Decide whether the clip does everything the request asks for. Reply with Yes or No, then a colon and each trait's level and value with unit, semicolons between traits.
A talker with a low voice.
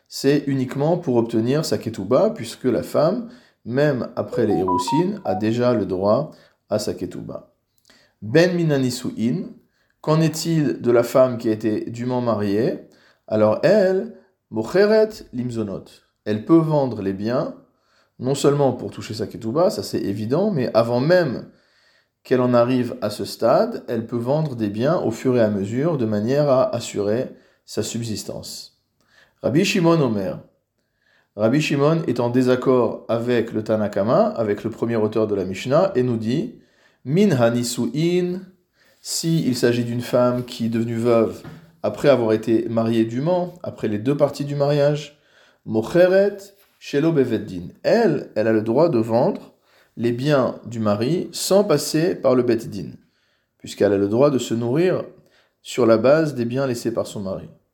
Yes: low, 125 Hz